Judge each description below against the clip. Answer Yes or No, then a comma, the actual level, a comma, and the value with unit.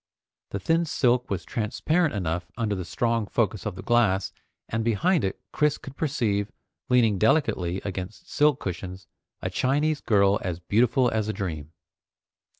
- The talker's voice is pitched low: Yes, low, 110 Hz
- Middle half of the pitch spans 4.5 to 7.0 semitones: Yes, average, 5.1 semitones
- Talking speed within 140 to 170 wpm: Yes, average, 150 wpm